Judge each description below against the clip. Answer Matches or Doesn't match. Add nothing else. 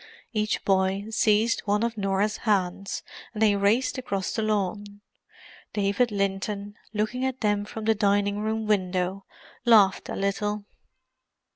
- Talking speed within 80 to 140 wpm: Matches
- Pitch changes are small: Matches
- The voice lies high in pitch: Matches